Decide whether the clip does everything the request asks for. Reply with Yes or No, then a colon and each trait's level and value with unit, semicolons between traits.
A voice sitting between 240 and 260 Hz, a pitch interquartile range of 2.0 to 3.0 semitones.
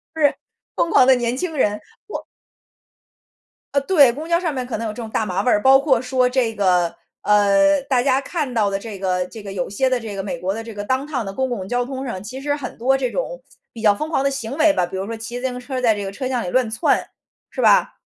No: high, 245 Hz; average, 4.6 semitones